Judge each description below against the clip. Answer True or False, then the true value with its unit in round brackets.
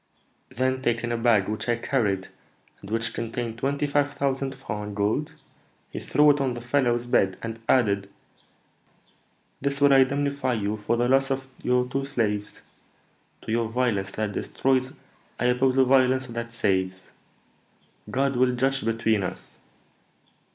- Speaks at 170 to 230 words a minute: False (150 wpm)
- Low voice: True (120 Hz)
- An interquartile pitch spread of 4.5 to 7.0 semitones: False (3.2 semitones)